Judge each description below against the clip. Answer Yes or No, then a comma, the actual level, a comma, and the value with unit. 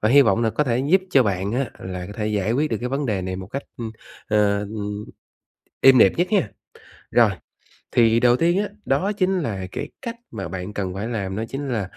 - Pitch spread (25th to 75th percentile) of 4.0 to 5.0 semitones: No, wide, 5.4 semitones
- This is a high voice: No, low, 115 Hz